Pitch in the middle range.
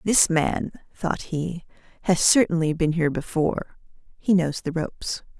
Yes: medium, 165 Hz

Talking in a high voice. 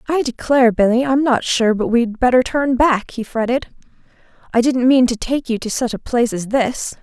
Yes: high, 245 Hz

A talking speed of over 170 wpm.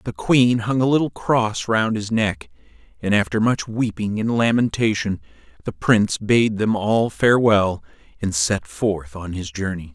No: average, 165 wpm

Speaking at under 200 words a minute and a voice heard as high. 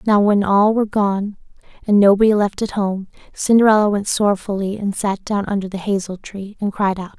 Yes: average, 190 wpm; high, 200 Hz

